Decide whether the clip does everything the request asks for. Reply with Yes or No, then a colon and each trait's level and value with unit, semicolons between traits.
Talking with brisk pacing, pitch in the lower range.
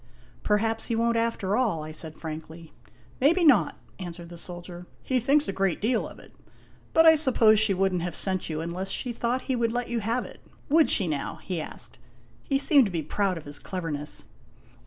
No: fast, 215 wpm; high, 195 Hz